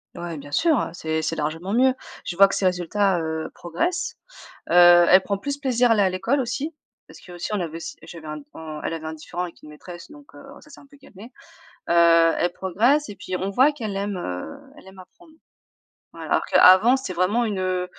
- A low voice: No, medium, 185 Hz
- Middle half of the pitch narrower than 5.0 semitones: No, wide, 6.1 semitones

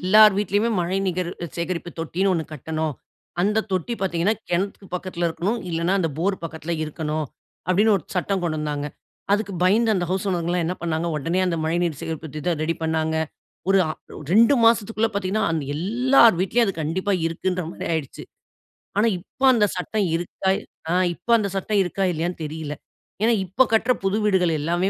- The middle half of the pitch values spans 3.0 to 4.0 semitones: Yes, average, 3.6 semitones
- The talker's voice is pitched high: No, medium, 180 Hz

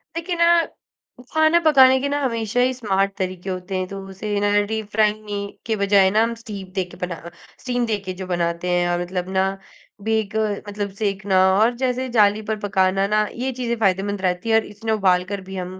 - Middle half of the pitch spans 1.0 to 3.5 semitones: Yes, average, 3.2 semitones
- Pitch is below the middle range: No, high, 205 Hz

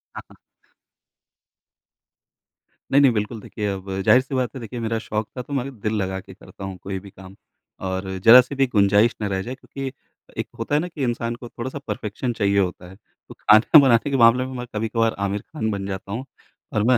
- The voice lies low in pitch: Yes, low, 115 Hz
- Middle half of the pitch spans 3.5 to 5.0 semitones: Yes, average, 4.2 semitones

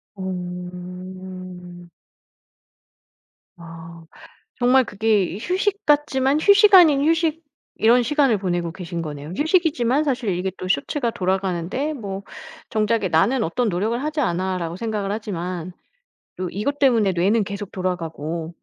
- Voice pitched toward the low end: No, high, 195 Hz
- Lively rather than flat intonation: Yes, wide, 6.6 semitones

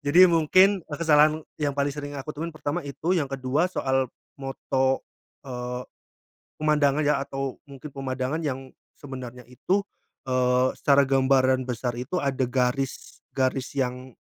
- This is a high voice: No, low, 135 Hz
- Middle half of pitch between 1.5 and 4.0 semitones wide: Yes, narrow, 2.4 semitones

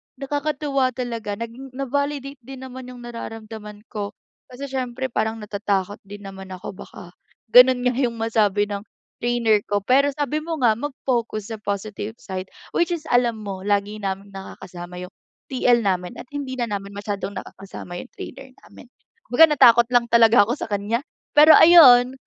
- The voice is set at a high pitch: Yes, high, 230 Hz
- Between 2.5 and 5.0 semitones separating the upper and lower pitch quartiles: Yes, average, 4.3 semitones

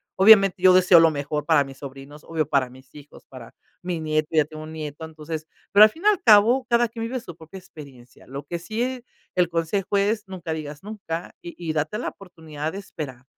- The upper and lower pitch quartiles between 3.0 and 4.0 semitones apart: No, average, 4.9 semitones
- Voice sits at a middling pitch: Yes, medium, 165 Hz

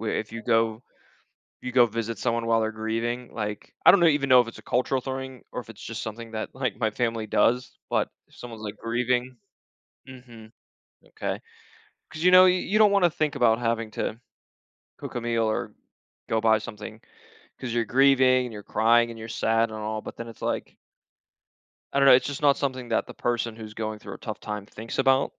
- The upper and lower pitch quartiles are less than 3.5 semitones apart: Yes, narrow, 2.5 semitones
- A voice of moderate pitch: No, low, 115 Hz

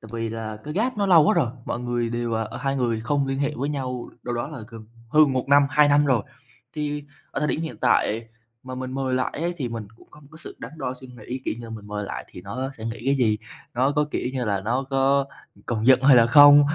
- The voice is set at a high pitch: No, low, 130 Hz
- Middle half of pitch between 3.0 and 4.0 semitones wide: Yes, average, 3.7 semitones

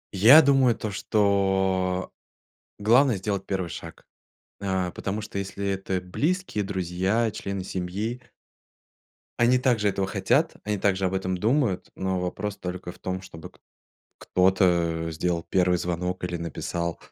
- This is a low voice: Yes, very low, 95 Hz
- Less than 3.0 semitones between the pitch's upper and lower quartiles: Yes, narrow, 2.4 semitones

